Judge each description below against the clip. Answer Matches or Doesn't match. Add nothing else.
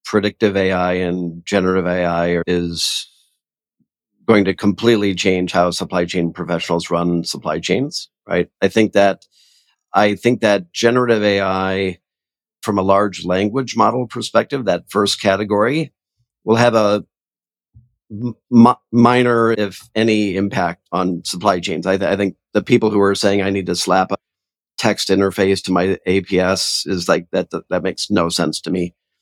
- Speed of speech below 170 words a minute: Matches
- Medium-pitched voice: Doesn't match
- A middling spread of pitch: Matches